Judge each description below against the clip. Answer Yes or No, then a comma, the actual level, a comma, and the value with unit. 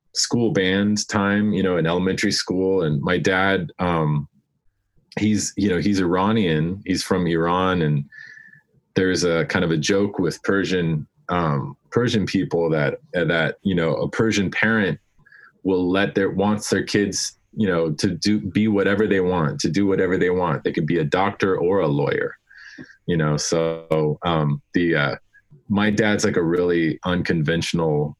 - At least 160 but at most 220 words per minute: Yes, average, 165 wpm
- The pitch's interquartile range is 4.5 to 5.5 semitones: No, average, 3.4 semitones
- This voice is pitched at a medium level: No, very low, 95 Hz